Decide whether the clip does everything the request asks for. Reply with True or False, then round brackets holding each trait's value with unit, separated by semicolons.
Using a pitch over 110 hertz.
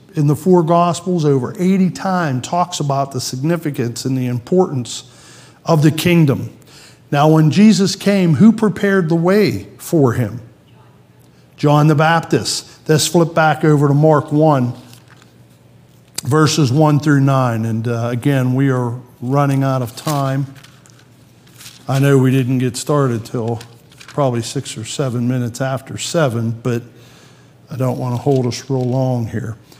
True (140 Hz)